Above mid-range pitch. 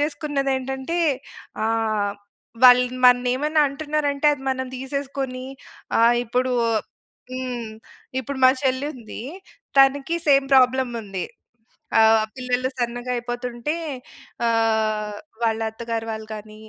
Yes: very high, 250 Hz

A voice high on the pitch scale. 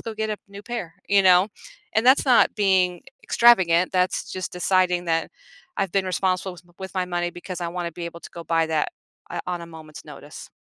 No: medium, 180 Hz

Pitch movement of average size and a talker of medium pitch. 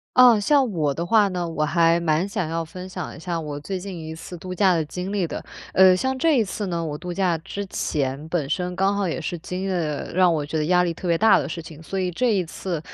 Yes: average, 3.0 semitones; medium, 180 Hz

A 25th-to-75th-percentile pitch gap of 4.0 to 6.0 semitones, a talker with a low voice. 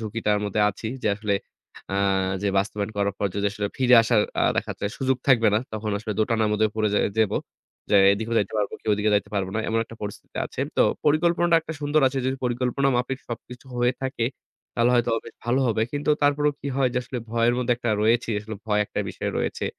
No: average, 3.3 semitones; low, 115 Hz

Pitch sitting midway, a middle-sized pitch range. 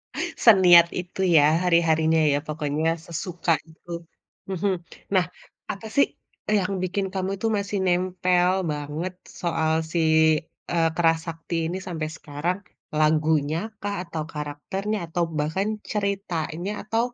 Yes: medium, 175 Hz; average, 3.2 semitones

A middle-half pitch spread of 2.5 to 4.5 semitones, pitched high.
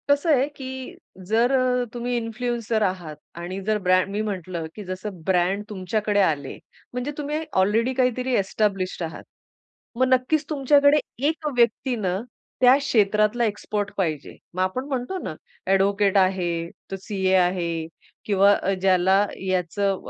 No: average, 5.0 semitones; high, 210 Hz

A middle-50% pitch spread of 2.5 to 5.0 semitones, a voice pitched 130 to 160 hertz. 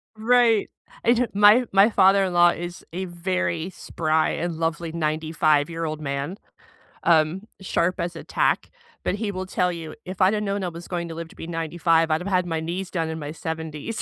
No: average, 2.8 semitones; medium, 170 Hz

